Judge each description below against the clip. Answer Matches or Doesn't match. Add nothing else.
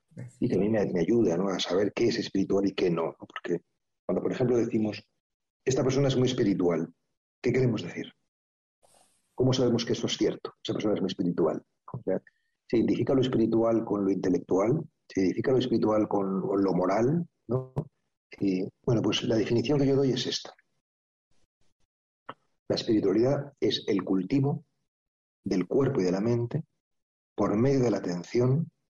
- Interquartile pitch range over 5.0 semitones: Matches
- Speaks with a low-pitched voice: Matches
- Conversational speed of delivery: Matches